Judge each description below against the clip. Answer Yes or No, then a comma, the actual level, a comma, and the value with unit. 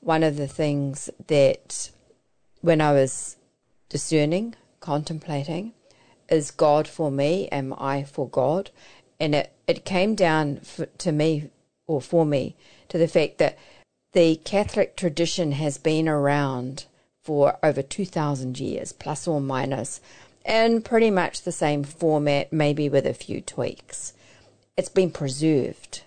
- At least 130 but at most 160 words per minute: Yes, average, 140 wpm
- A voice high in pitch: No, medium, 150 Hz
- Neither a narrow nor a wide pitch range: Yes, average, 3.2 semitones